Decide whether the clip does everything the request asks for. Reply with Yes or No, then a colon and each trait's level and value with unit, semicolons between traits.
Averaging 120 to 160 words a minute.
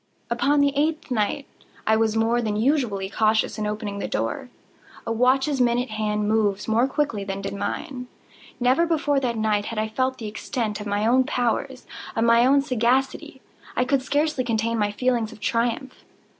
No: average, 170 wpm